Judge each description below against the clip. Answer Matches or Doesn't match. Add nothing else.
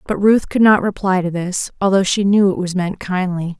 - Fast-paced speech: Matches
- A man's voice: Doesn't match